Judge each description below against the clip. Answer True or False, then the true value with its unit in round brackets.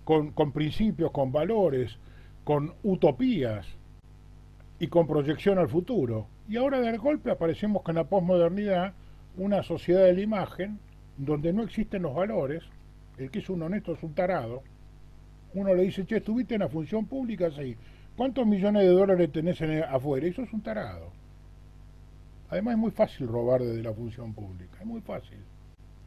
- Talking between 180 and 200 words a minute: False (165 wpm)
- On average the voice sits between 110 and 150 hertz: False (165 Hz)